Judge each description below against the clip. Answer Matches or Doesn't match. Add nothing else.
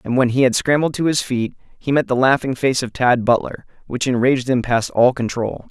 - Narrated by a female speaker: Doesn't match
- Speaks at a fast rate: Matches